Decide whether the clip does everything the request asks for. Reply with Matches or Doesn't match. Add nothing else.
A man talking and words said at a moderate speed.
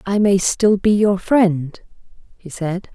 Doesn't match